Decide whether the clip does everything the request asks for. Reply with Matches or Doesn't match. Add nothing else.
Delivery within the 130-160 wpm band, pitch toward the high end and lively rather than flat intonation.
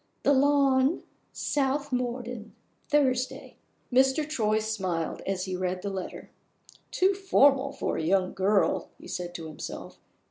Matches